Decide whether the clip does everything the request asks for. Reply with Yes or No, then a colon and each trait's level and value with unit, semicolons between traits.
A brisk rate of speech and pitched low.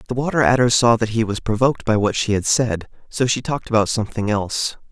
Yes: fast, 230 wpm; low, 115 Hz